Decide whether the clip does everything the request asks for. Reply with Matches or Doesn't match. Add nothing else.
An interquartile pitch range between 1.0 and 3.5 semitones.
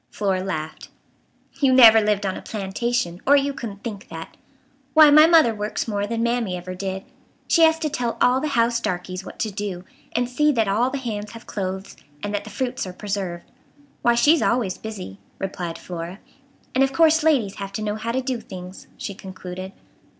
Doesn't match